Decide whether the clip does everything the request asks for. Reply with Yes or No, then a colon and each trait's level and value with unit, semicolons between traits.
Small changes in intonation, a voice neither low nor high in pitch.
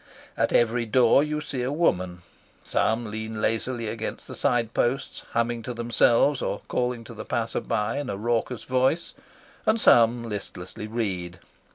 No: narrow, 2.2 semitones; low, 115 Hz